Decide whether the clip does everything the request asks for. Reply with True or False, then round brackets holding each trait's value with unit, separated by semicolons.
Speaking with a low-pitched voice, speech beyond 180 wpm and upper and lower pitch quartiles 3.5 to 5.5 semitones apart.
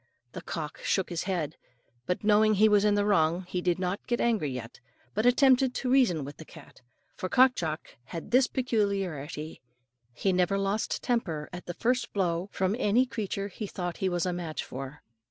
False (190 Hz; 190 wpm; 4.5 semitones)